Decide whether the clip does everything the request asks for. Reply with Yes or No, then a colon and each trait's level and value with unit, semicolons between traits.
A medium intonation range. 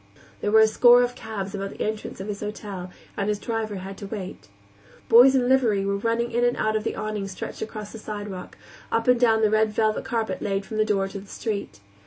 No: narrow, 2.3 semitones